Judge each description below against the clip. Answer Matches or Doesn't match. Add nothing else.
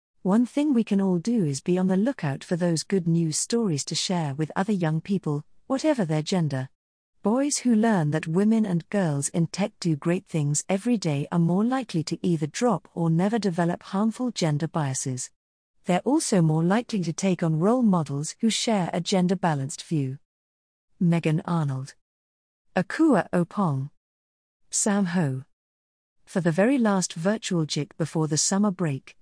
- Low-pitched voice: Doesn't match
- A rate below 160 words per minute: Doesn't match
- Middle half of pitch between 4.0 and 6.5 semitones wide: Matches